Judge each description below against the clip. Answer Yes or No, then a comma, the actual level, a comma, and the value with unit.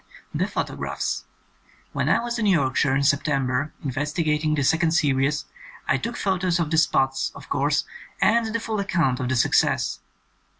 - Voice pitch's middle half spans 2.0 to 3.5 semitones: No, average, 4.8 semitones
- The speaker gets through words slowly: No, average, 170 wpm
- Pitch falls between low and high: Yes, medium, 150 Hz